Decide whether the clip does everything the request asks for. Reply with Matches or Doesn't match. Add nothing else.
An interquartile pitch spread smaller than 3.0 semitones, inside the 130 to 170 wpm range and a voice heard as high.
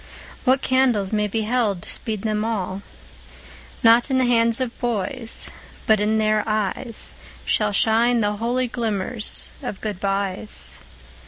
Matches